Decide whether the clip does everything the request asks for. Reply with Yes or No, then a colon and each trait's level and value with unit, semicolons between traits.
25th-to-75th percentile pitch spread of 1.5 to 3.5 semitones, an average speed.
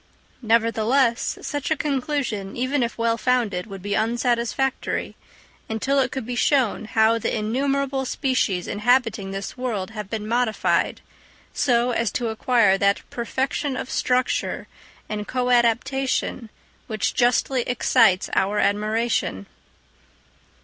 No: average, 3.1 semitones; slow, 120 wpm